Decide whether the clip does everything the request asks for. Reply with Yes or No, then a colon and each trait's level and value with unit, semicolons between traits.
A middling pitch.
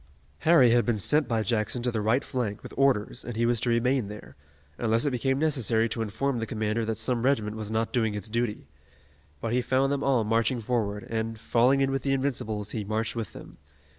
No: low, 115 Hz